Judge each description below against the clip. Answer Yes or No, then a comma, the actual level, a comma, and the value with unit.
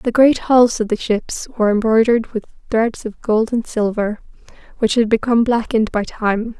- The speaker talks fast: No, average, 180 wpm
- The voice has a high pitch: Yes, high, 225 Hz